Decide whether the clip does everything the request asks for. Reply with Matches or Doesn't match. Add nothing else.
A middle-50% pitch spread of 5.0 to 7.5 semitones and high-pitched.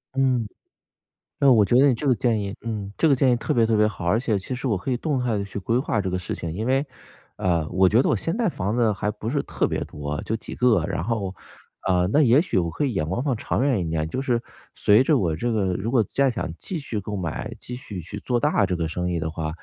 Doesn't match